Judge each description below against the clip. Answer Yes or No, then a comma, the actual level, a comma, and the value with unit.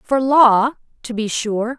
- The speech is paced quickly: No, average, 170 wpm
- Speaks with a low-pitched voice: No, high, 240 Hz